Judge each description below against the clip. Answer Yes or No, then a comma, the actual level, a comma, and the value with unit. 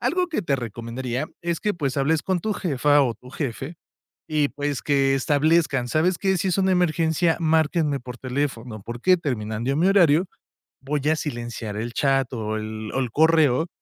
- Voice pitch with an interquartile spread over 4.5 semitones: Yes, average, 5.0 semitones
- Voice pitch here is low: No, medium, 145 Hz